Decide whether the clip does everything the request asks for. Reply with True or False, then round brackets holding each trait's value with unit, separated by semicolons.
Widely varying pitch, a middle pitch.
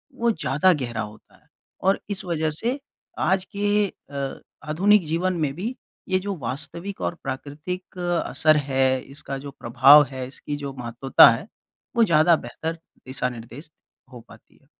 True (5.9 semitones; 150 Hz)